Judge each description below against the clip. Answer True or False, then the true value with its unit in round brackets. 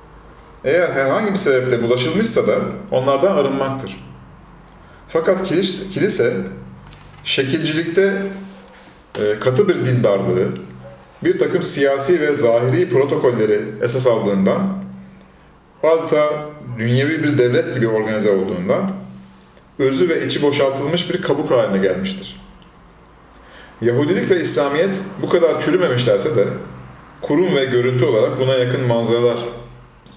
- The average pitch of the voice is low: True (125 Hz)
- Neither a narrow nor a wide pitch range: False (7.0 semitones)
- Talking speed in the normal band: True (105 wpm)